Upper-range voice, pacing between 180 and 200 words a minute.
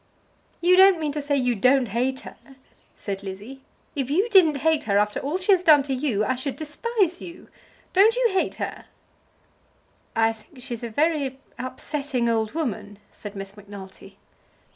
No: very high, 270 Hz; average, 170 wpm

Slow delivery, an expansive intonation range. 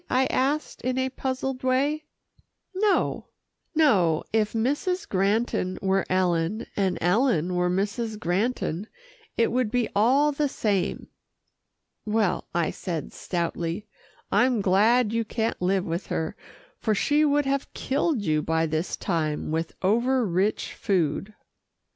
Yes: slow, 130 wpm; wide, 6.3 semitones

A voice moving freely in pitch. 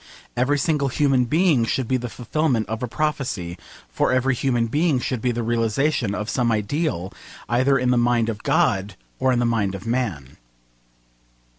No: average, 3.4 semitones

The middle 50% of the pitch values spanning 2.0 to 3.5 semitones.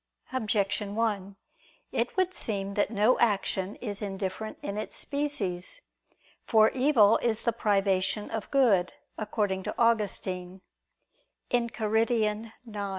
Yes: average, 2.8 semitones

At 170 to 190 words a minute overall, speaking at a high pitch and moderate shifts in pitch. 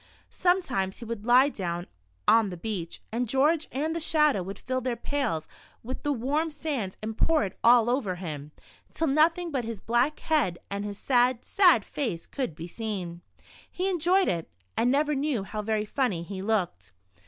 No: average, 180 wpm; high, 240 Hz; wide, 7.0 semitones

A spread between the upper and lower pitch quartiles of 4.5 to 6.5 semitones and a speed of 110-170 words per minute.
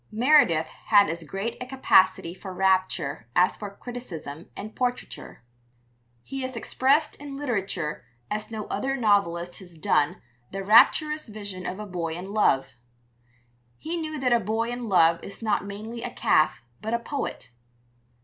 Yes: wide, 5.4 semitones; average, 155 wpm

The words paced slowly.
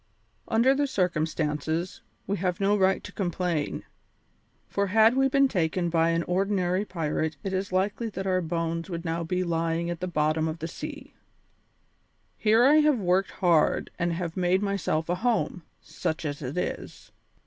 No: average, 170 wpm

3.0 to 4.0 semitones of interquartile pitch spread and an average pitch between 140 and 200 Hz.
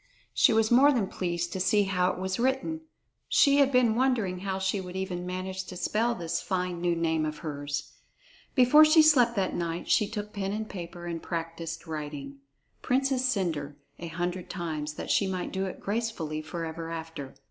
No: average, 4.8 semitones; medium, 185 Hz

